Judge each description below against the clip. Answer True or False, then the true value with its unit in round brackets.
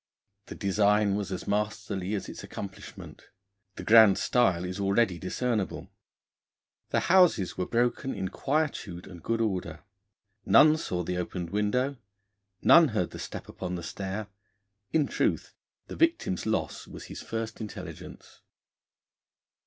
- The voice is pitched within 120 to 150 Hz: False (105 Hz)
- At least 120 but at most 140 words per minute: True (135 wpm)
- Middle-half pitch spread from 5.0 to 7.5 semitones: False (4.2 semitones)